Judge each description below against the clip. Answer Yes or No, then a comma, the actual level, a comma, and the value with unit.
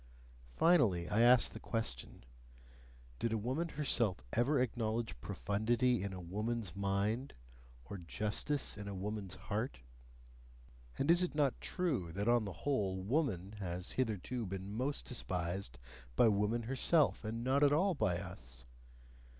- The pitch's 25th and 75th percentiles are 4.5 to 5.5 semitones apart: Yes, average, 5.1 semitones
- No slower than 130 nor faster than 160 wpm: Yes, average, 140 wpm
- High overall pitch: No, low, 110 Hz